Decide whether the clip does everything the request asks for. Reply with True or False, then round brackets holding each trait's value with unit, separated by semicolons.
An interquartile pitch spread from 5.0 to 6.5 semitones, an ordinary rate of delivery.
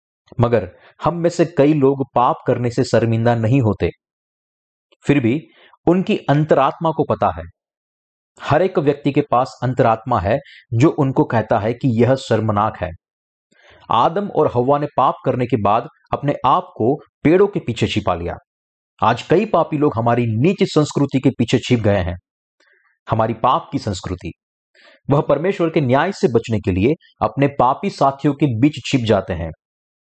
True (5.6 semitones; 165 wpm)